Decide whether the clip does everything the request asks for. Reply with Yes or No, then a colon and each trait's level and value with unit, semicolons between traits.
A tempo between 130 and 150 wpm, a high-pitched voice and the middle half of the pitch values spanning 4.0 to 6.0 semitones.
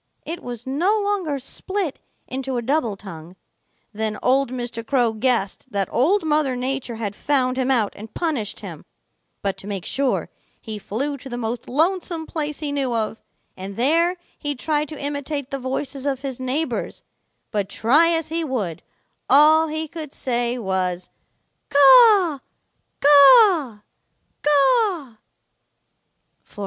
Yes: average, 140 wpm; very high, 270 Hz; average, 4.8 semitones